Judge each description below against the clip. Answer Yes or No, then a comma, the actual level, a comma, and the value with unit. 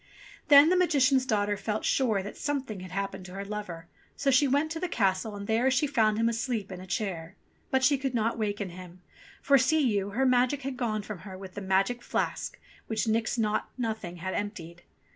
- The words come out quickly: Yes, fast, 215 wpm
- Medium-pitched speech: No, high, 220 Hz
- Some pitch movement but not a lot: Yes, average, 4.9 semitones